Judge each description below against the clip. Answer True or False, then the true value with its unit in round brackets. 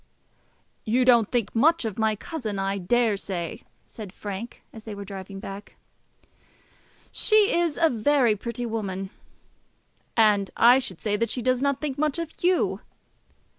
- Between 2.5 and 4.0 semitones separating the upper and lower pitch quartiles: False (4.4 semitones)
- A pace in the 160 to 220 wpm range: False (150 wpm)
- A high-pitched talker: True (225 Hz)